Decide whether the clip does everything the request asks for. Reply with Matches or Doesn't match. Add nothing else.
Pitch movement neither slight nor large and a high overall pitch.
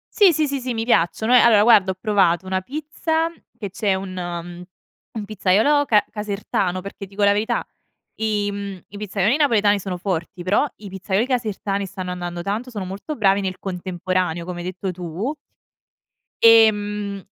Matches